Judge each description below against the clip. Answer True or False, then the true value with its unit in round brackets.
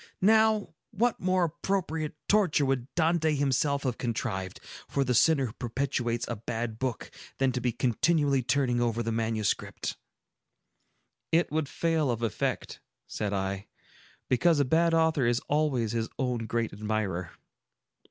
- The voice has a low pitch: True (130 Hz)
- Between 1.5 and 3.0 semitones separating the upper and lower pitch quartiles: False (5.5 semitones)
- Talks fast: False (145 wpm)